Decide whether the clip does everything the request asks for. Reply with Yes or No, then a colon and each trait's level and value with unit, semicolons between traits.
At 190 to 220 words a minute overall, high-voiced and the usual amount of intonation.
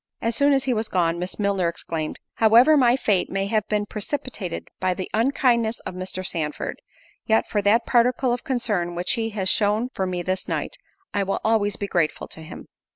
Yes: average, 200 wpm; high, 205 Hz; average, 4.1 semitones